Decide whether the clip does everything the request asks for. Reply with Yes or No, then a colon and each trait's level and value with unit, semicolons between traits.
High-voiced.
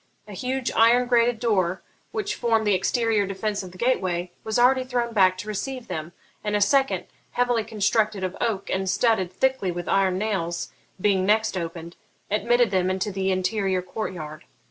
Yes: high, 205 Hz